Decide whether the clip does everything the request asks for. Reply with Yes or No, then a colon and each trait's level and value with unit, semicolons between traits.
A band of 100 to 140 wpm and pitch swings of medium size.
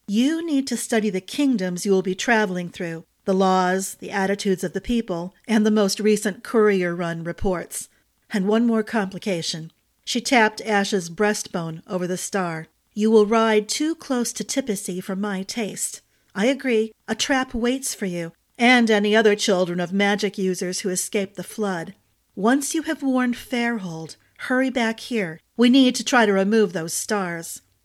No: average, 170 wpm; average, 4.0 semitones